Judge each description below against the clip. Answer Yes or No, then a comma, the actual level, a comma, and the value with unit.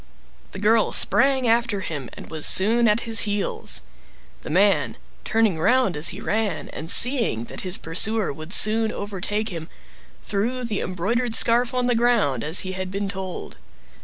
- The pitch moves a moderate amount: Yes, average, 3.9 semitones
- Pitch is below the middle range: No, high, 205 Hz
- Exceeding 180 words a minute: No, average, 165 wpm